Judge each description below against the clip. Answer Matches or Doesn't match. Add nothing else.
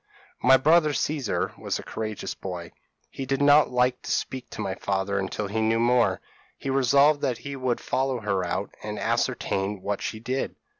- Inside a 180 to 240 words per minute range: Matches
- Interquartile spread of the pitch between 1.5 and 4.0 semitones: Doesn't match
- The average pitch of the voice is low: Matches